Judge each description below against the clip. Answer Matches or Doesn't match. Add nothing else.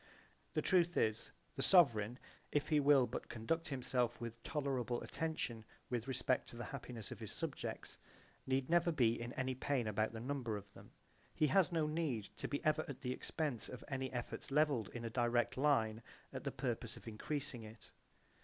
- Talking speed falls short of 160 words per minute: Doesn't match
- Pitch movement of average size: Matches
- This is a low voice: Matches